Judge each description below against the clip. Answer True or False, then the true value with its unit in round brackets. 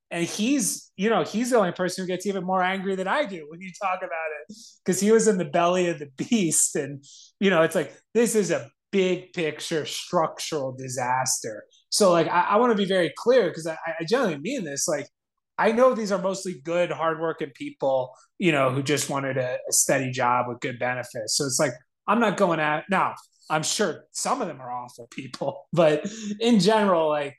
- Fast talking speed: True (215 wpm)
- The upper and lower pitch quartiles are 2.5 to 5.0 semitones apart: False (5.5 semitones)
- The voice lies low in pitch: False (175 Hz)